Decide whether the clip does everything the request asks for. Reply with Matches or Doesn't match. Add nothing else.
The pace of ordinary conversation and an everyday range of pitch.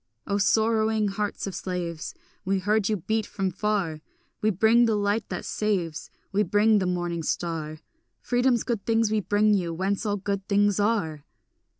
Matches